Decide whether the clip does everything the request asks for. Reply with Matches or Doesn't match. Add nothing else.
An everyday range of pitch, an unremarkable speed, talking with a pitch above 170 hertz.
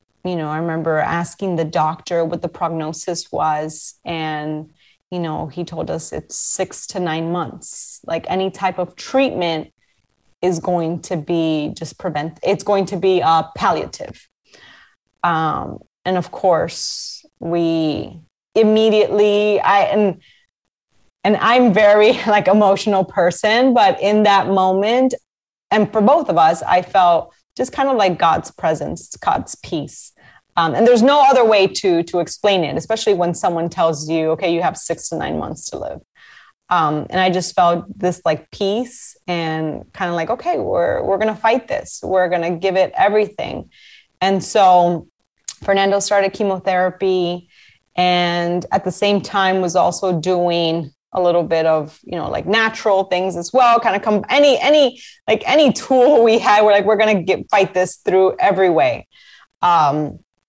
Matches